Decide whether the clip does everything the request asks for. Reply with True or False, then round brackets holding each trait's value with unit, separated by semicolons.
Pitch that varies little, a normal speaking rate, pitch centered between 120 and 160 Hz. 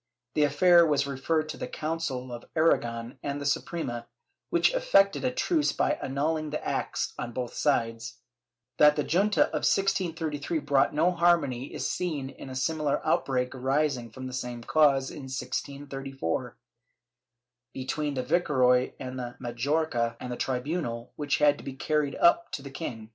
False (3.8 semitones; 160 wpm; 140 Hz)